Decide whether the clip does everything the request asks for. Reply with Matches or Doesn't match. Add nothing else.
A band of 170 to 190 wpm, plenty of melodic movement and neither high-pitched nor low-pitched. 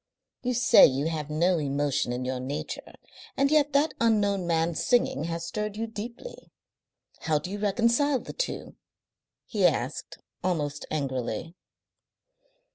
Doesn't match